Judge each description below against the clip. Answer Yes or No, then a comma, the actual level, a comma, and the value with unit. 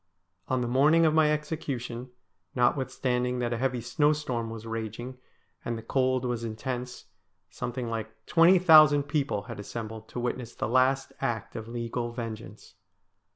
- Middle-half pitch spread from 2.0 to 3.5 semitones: Yes, average, 2.9 semitones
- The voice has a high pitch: No, low, 125 Hz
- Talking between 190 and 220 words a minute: No, average, 155 wpm